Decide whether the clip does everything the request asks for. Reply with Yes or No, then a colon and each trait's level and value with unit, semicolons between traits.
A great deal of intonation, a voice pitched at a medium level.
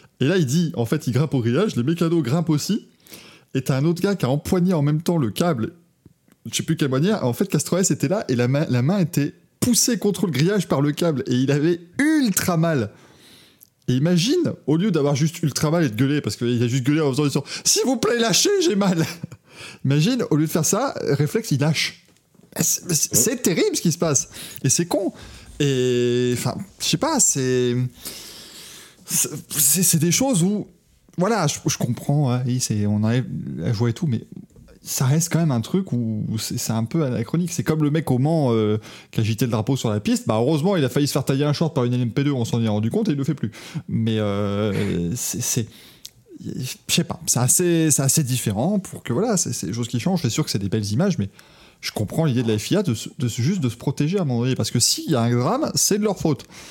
Yes: wide, 5.7 semitones; medium, 145 Hz